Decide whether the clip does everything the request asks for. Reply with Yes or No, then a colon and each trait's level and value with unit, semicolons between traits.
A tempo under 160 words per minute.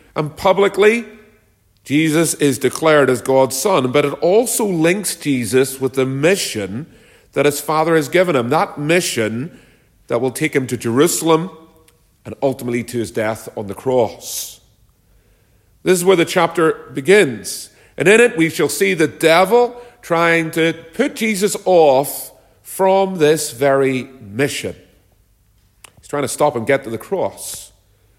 Yes: average, 150 wpm